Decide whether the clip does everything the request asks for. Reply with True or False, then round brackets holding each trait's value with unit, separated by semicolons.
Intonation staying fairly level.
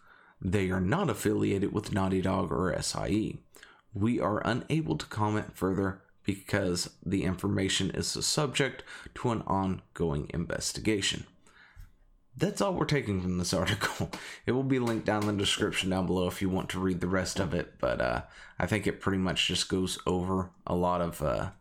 True (2.0 semitones)